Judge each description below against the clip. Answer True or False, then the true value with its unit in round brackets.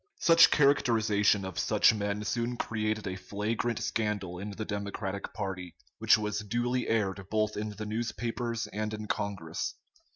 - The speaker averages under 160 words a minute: True (150 wpm)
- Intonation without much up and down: True (2.0 semitones)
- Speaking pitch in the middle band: False (105 Hz)